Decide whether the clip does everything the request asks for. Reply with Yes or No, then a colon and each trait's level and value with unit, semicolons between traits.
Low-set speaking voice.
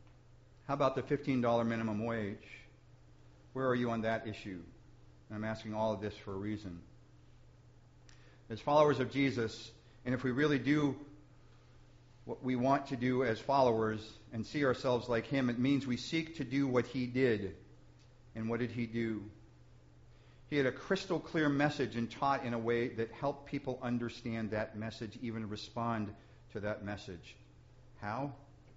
Yes: low, 120 Hz